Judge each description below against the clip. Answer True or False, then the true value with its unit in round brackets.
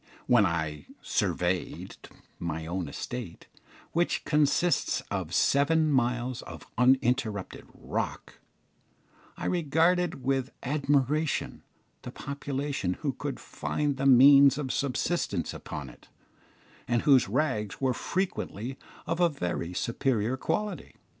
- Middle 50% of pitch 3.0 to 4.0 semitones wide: False (5.3 semitones)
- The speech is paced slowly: True (110 wpm)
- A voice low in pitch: True (130 Hz)